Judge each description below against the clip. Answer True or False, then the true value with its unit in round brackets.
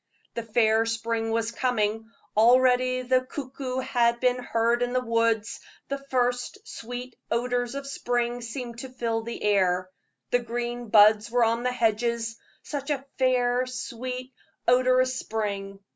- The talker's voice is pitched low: False (240 Hz)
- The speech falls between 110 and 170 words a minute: True (145 wpm)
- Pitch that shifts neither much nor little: False (1.9 semitones)